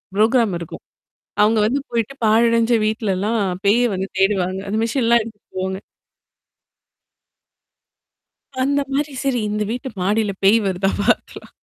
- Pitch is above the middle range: Yes, high, 220 Hz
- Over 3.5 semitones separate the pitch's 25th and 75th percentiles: No, average, 3.2 semitones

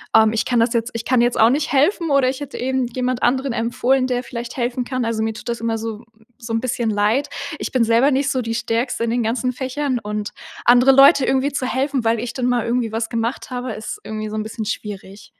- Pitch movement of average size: No, narrow, 2.3 semitones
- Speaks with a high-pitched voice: Yes, high, 240 Hz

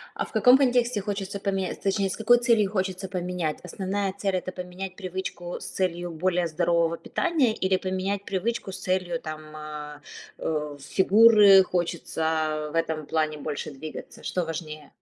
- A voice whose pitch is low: No, medium, 185 Hz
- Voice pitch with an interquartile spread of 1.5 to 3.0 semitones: No, average, 3.5 semitones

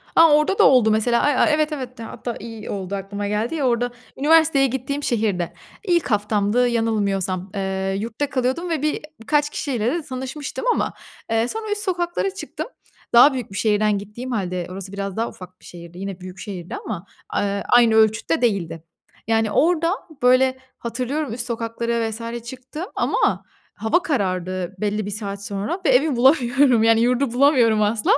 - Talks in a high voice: Yes, high, 230 Hz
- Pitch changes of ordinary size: Yes, average, 5.0 semitones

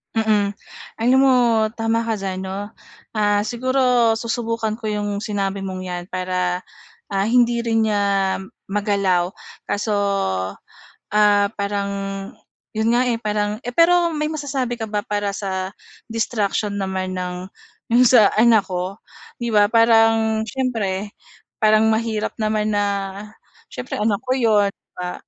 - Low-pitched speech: No, high, 210 Hz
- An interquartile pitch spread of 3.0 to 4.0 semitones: No, narrow, 2.5 semitones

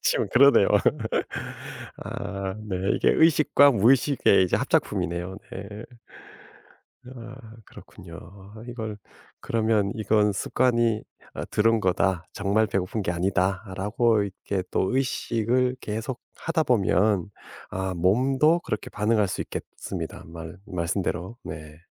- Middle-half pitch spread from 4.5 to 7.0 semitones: No, average, 3.9 semitones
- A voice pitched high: No, low, 105 Hz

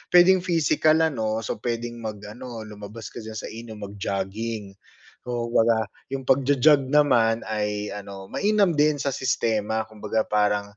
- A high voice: No, low, 115 Hz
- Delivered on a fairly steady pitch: No, average, 4.2 semitones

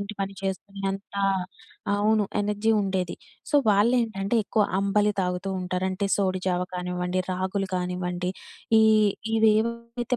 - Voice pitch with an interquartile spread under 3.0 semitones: Yes, narrow, 2.4 semitones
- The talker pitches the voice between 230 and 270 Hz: No, high, 195 Hz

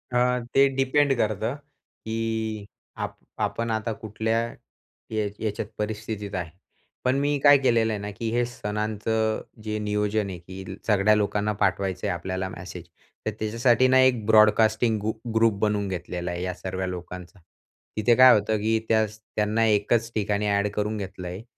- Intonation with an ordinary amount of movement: No, narrow, 2.0 semitones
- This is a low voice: Yes, low, 105 Hz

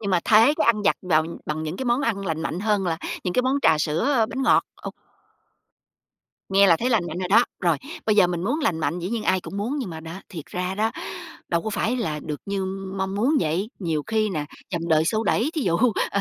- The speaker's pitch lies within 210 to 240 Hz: No, high, 195 Hz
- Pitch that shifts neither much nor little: Yes, average, 4.9 semitones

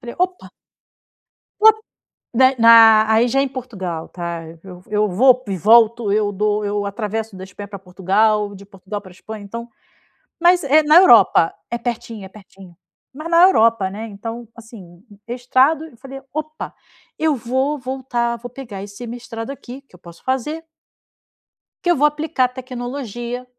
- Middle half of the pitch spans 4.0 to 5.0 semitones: Yes, average, 4.4 semitones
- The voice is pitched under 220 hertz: No, high, 230 Hz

